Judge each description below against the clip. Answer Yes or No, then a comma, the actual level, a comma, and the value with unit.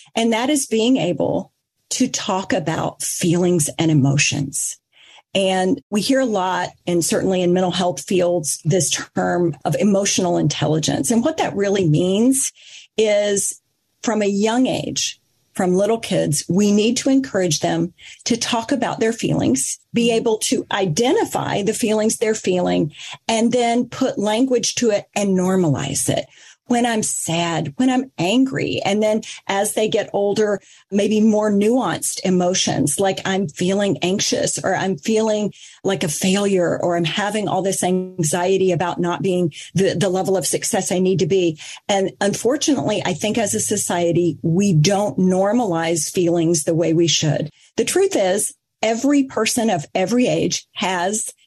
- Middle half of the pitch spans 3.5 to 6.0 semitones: Yes, average, 4.0 semitones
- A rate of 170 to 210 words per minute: No, average, 155 wpm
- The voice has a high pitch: Yes, high, 195 Hz